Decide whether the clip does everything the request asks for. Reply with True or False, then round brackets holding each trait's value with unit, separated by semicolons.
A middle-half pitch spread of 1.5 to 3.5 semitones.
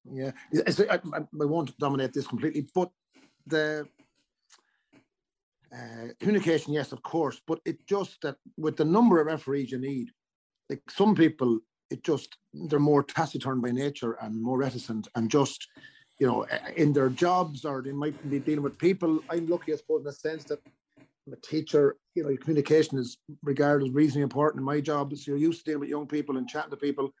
True (2.5 semitones)